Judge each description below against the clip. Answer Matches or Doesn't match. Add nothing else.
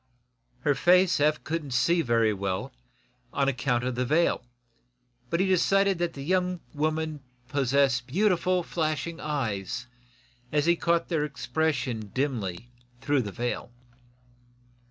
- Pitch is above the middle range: Doesn't match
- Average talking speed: Doesn't match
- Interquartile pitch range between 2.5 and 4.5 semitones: Doesn't match